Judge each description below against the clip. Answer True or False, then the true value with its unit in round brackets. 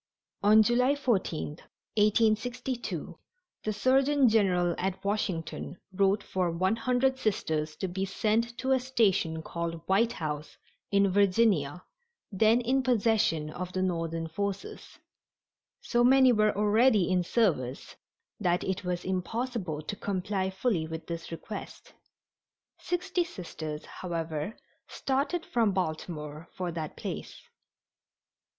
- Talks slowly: True (120 wpm)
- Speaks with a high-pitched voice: True (195 Hz)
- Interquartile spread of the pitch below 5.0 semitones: False (5.5 semitones)